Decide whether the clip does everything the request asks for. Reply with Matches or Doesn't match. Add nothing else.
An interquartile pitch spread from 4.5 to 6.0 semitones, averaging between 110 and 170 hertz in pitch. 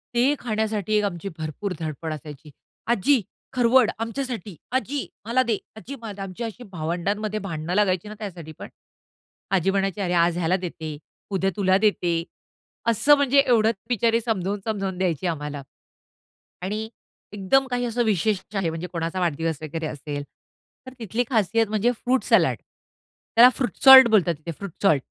Doesn't match